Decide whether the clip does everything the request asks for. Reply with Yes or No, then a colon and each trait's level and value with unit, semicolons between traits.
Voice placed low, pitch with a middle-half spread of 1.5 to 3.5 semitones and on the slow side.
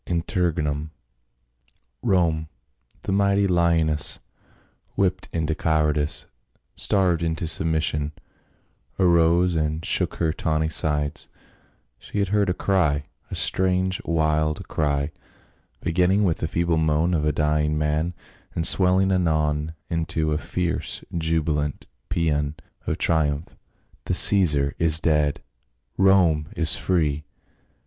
Yes: very low, 80 Hz; average, 2.7 semitones; slow, 115 wpm